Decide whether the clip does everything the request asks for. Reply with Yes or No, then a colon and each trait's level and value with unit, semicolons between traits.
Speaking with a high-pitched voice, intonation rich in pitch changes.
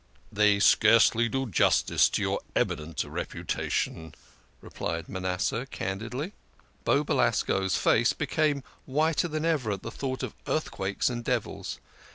No: low, 115 Hz; wide, 6.1 semitones